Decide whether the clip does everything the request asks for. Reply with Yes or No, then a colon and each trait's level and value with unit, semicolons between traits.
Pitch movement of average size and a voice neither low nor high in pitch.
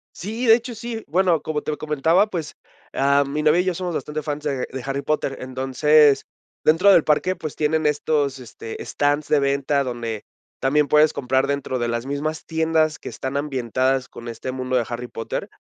Yes: average, 3.0 semitones; medium, 145 Hz